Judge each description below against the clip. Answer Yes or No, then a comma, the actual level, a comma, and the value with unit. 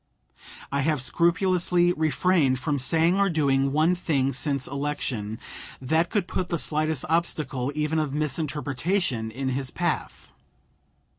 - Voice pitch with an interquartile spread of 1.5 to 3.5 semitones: No, average, 3.9 semitones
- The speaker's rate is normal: No, slow, 130 wpm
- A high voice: No, medium, 150 Hz